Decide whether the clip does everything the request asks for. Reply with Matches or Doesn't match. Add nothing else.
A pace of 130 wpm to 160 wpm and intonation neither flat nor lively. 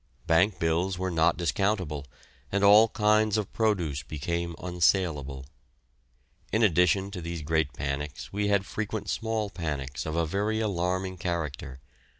Matches